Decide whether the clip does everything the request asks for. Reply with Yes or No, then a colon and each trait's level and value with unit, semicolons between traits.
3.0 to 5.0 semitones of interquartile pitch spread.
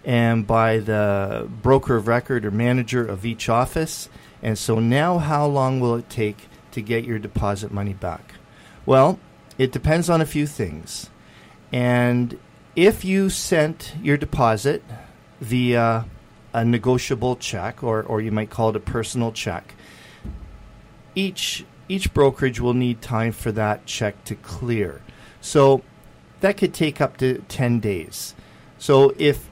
Yes: average, 3.9 semitones